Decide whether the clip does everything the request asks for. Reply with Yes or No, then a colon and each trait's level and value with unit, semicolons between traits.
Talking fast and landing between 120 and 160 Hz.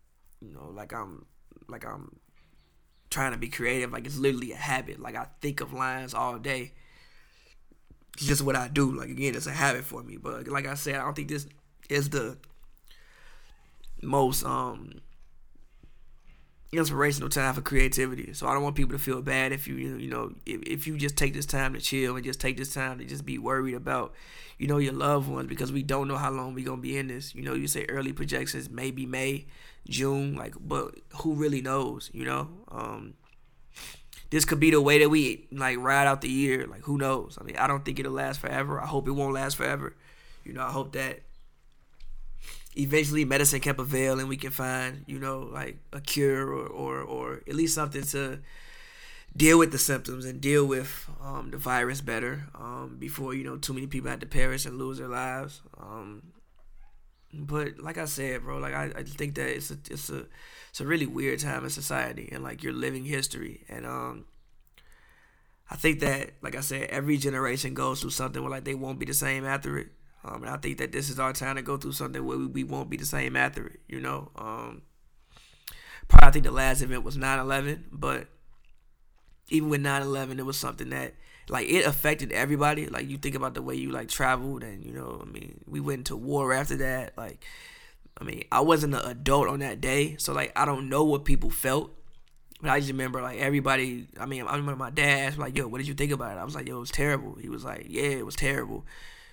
Yes: fast, 220 wpm; low, 135 Hz